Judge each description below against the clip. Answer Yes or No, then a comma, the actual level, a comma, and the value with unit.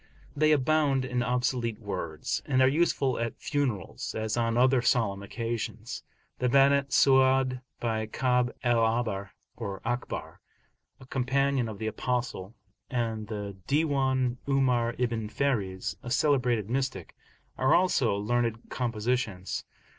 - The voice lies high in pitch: No, low, 120 Hz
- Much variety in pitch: No, average, 3.1 semitones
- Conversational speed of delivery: No, slow, 125 wpm